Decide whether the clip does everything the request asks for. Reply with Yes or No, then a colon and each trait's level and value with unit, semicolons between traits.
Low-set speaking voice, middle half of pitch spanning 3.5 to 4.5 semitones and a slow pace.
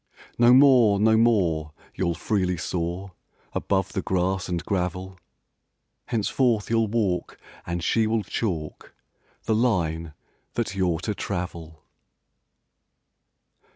Yes: very low, 95 Hz; average, 4.2 semitones; slow, 110 wpm